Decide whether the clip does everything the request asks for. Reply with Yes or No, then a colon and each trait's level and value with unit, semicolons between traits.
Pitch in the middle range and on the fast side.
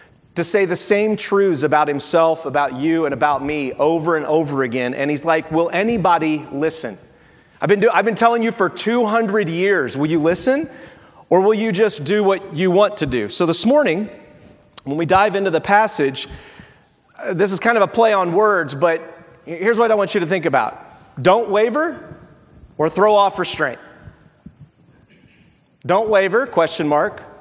No: medium, 180 Hz; average, 175 wpm